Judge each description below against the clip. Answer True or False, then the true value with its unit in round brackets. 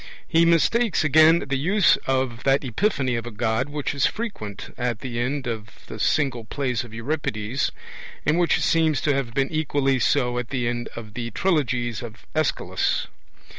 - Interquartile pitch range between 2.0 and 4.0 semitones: False (4.6 semitones)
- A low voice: True (130 Hz)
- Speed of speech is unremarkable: True (170 wpm)